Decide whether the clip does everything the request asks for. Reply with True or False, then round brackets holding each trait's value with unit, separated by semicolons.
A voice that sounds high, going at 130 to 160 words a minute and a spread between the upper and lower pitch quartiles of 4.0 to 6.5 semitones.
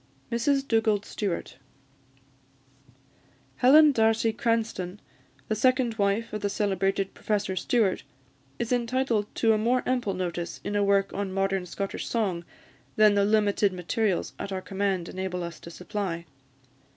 False (205 Hz; 140 wpm; 3.1 semitones)